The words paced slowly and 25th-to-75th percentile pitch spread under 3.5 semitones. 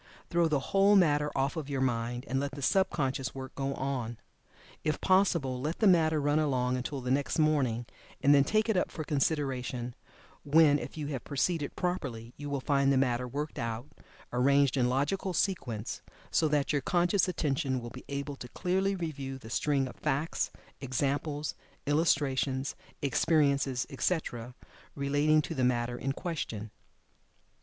No: average, 165 wpm; average, 3.0 semitones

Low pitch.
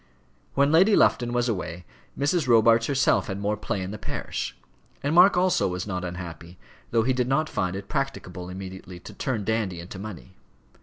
Yes: low, 105 Hz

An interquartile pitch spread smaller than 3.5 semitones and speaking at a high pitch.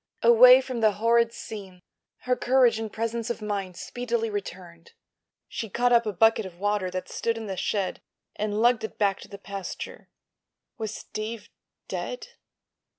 Yes: average, 2.7 semitones; high, 220 Hz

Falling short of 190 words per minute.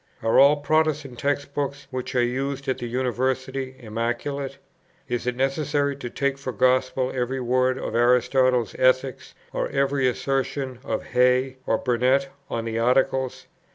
Yes: average, 150 wpm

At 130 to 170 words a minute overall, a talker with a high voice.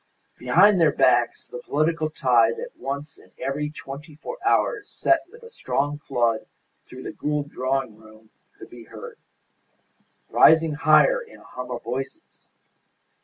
No: average, 150 wpm; medium, 145 Hz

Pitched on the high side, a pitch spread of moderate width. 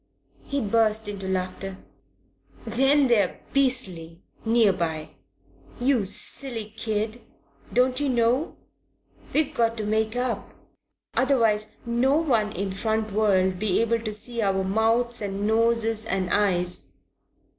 Yes: high, 220 Hz; average, 3.2 semitones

